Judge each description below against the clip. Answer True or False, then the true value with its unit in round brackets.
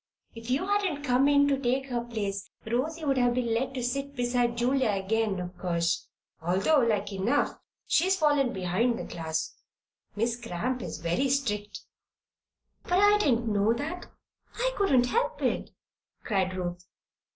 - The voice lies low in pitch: False (240 Hz)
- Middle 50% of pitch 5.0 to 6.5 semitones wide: True (5.5 semitones)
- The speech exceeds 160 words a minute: False (150 wpm)